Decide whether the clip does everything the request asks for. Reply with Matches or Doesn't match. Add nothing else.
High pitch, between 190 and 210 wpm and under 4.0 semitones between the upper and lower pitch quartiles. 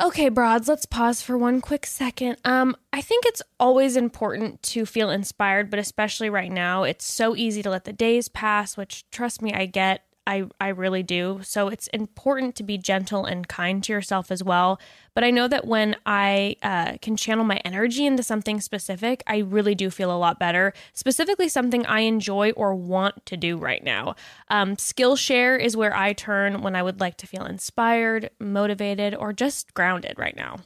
Matches